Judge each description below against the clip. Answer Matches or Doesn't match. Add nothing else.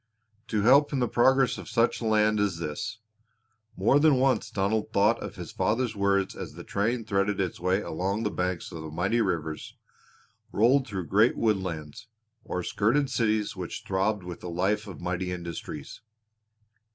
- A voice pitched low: Matches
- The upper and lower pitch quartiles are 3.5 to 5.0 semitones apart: Matches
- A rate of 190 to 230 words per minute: Doesn't match